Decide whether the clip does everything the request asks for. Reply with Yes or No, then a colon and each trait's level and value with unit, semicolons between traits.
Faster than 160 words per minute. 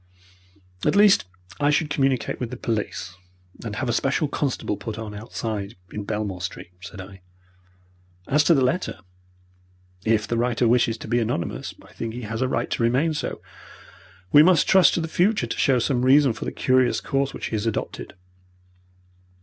Yes: average, 180 wpm